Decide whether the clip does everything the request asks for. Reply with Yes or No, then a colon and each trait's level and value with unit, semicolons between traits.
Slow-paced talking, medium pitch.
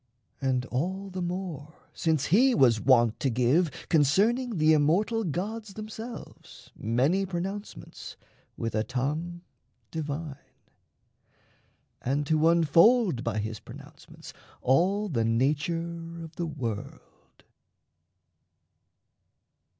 Yes: slow, 100 wpm; medium, 160 Hz